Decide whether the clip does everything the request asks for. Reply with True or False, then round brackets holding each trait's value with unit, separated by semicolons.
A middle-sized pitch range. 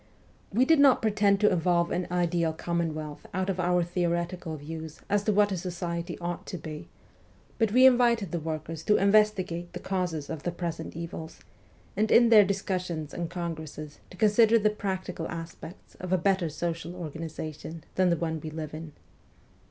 True (3.3 semitones)